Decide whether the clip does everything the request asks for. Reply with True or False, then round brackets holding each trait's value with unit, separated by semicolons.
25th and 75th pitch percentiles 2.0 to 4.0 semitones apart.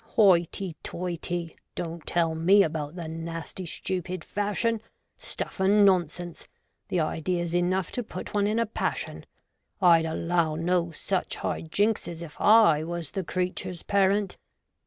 True (2.8 semitones)